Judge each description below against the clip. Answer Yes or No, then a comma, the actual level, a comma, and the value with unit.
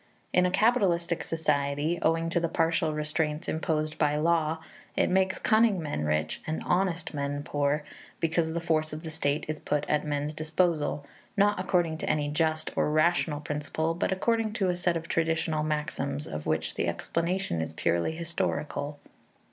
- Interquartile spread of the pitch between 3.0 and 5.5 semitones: No, narrow, 2.4 semitones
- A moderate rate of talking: Yes, average, 170 wpm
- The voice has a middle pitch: Yes, medium, 160 Hz